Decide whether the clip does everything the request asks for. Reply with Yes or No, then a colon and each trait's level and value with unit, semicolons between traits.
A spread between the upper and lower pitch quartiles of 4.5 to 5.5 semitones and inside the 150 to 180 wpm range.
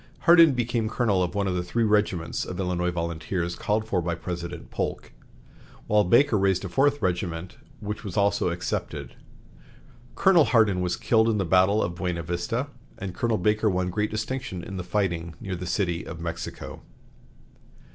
No: average, 3.7 semitones; average, 170 wpm